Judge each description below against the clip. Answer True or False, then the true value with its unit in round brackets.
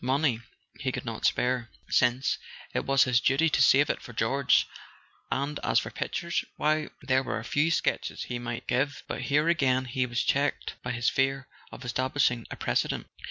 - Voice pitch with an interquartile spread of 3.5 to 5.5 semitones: False (2.5 semitones)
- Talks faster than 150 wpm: True (180 wpm)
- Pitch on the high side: False (130 Hz)